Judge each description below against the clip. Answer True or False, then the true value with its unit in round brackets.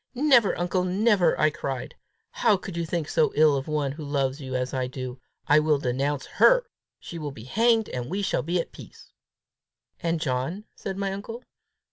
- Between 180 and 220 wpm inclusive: True (190 wpm)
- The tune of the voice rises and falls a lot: True (6.2 semitones)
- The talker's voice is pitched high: False (155 Hz)